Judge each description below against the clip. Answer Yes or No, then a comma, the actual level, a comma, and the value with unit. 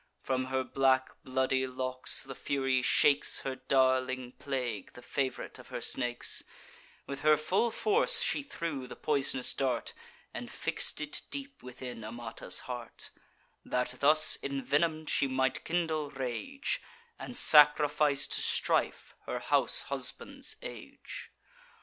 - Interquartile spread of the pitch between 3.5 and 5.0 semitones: No, average, 2.9 semitones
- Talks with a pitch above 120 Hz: Yes, low, 135 Hz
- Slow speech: Yes, slow, 130 wpm